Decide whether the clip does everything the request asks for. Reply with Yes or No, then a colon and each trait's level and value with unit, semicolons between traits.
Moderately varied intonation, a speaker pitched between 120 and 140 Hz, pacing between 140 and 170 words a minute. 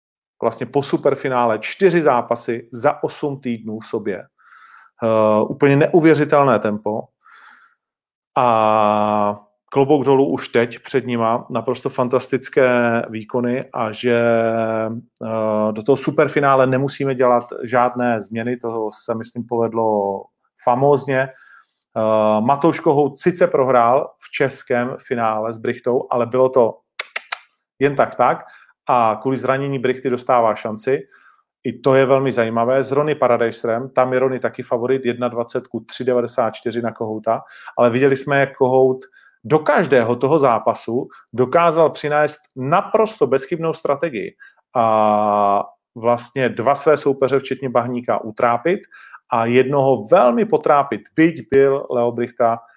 No: average, 3.0 semitones; low, 125 Hz; average, 125 wpm